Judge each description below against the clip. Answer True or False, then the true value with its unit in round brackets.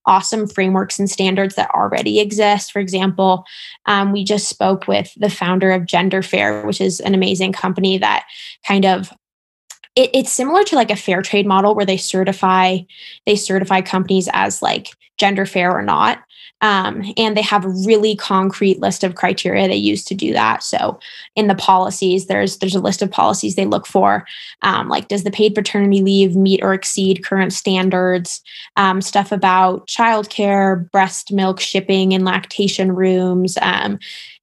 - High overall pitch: True (195 Hz)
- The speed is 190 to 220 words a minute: False (175 wpm)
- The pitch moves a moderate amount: False (1.3 semitones)